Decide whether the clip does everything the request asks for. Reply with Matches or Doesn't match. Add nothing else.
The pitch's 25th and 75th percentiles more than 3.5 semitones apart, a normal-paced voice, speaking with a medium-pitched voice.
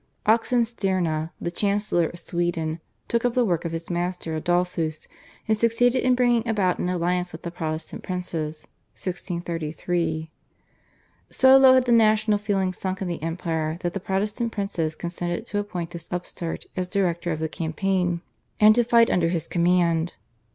Matches